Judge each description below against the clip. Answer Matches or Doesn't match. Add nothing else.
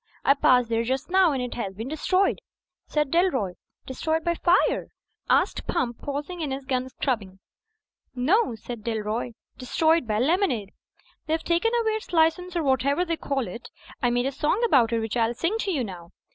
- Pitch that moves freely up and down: Matches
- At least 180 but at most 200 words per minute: Matches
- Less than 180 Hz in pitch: Doesn't match